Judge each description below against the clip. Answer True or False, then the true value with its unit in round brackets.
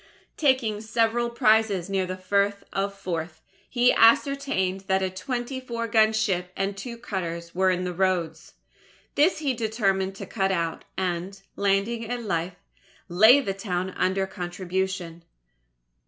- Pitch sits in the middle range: False (195 Hz)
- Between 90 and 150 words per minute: True (140 wpm)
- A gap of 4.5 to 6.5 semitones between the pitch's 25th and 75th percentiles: False (3.6 semitones)